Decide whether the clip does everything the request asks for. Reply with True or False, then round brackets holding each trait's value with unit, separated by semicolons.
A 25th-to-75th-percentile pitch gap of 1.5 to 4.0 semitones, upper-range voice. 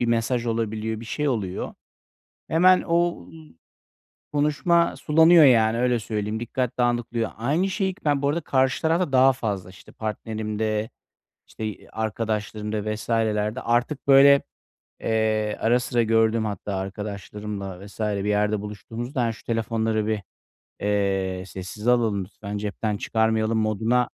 False (2.8 semitones; 110 Hz)